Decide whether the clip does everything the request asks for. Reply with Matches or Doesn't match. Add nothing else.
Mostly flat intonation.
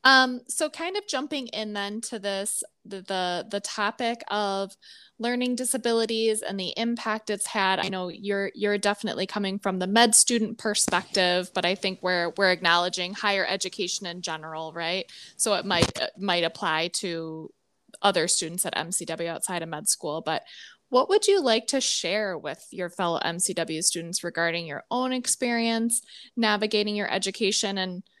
Doesn't match